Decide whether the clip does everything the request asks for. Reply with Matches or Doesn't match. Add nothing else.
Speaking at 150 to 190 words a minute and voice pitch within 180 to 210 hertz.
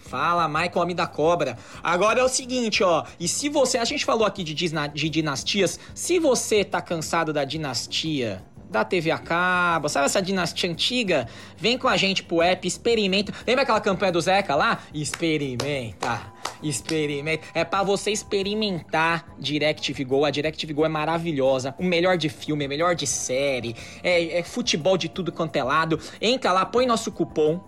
Doesn't match